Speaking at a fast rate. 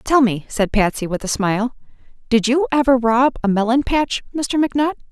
No: average, 190 wpm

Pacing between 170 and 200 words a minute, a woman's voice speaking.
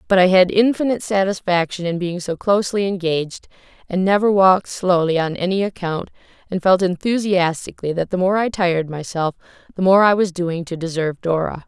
Yes: average, 175 wpm; female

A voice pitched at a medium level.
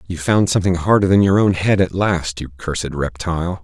No: very low, 90 Hz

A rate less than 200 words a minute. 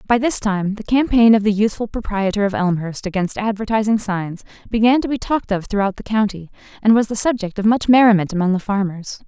No: fast, 205 wpm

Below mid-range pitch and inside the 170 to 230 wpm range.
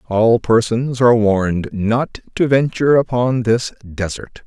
No: low, 115 Hz; slow, 135 wpm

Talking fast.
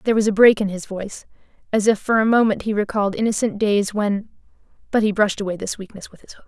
Yes: fast, 230 wpm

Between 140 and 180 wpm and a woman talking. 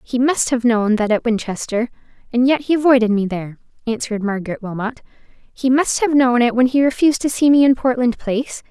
No: fast, 205 wpm; female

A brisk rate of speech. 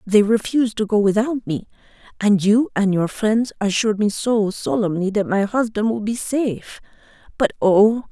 No: average, 170 wpm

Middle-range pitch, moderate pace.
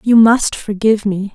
No: high, 210 Hz; average, 180 wpm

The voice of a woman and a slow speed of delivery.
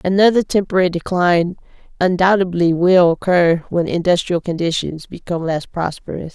Yes: female; slow, 115 wpm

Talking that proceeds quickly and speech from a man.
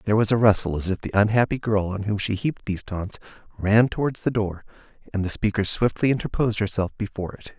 Yes: fast, 215 wpm; male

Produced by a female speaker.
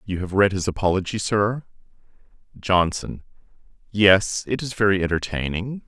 No: male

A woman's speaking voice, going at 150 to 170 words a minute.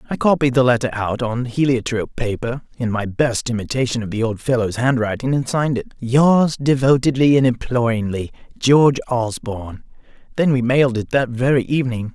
No: male; average, 165 wpm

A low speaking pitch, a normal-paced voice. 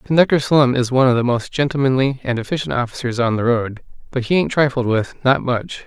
No: low, 130 Hz; fast, 215 wpm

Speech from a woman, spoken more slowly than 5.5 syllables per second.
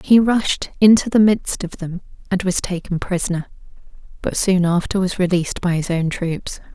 Yes: female; 5.0 syllables/s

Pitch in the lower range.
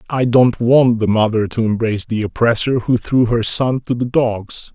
Yes: low, 115 Hz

